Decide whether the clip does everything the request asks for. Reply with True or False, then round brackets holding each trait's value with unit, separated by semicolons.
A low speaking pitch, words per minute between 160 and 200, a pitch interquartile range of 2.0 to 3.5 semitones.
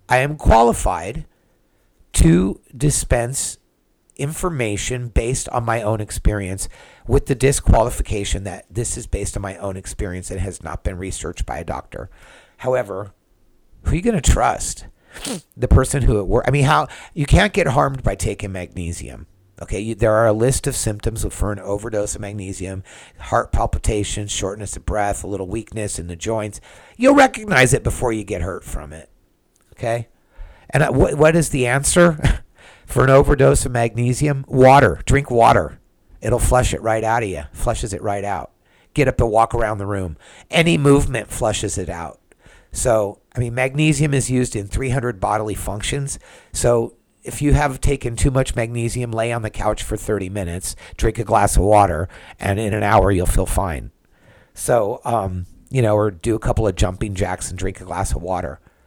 False (110 Hz; 180 wpm; 4.6 semitones)